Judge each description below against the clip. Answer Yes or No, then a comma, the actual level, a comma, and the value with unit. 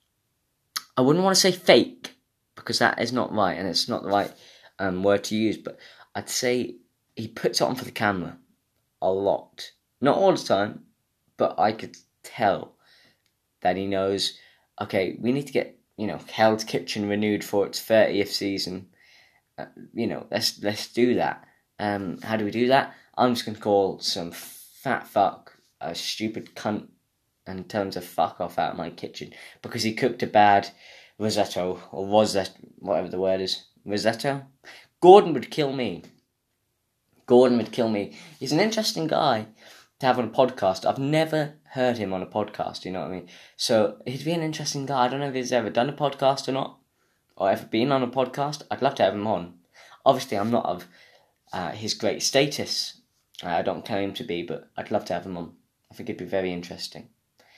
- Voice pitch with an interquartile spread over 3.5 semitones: Yes, average, 4.6 semitones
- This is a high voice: No, low, 110 Hz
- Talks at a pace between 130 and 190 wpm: No, average, 200 wpm